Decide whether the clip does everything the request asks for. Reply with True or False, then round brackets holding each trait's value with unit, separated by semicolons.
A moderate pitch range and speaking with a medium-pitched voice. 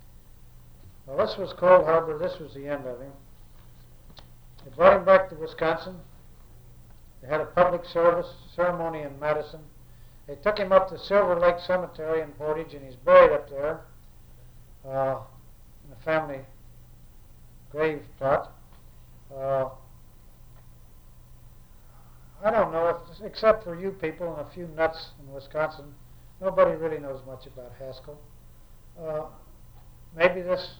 False (6.3 semitones; 150 Hz)